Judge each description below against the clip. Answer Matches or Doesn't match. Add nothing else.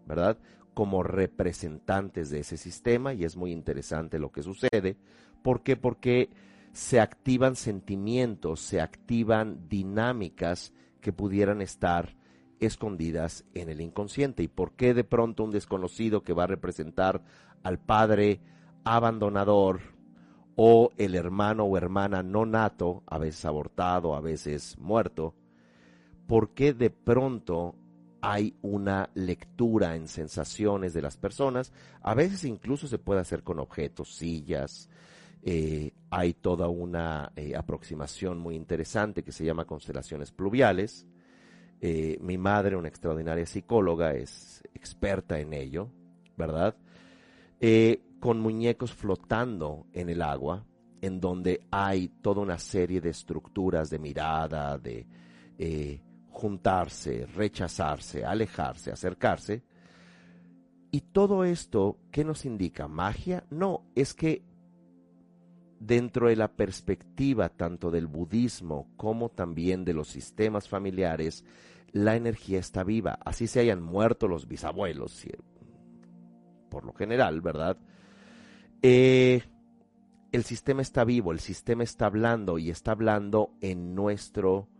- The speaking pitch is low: Matches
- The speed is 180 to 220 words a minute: Doesn't match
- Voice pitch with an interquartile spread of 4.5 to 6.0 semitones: Matches